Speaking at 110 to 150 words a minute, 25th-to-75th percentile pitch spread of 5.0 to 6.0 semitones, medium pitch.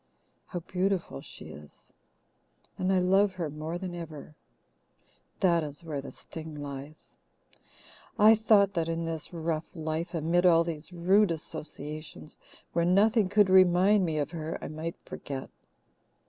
No: average, 145 wpm; average, 3.2 semitones; medium, 170 Hz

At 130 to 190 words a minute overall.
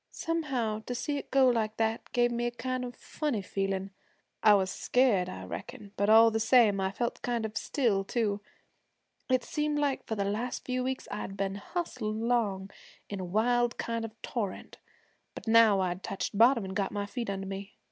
No: average, 200 wpm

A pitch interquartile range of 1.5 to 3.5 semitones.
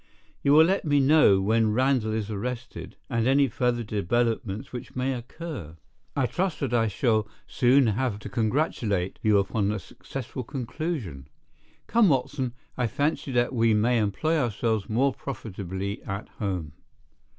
No: average, 4.2 semitones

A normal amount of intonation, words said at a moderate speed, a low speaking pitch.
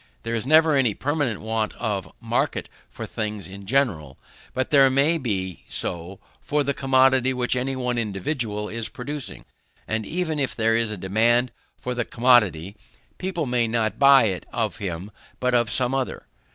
Yes: average, 4.0 semitones; average, 170 wpm; low, 120 Hz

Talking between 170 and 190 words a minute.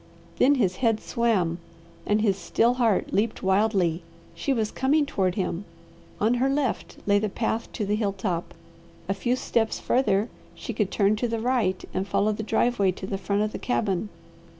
Yes: average, 185 wpm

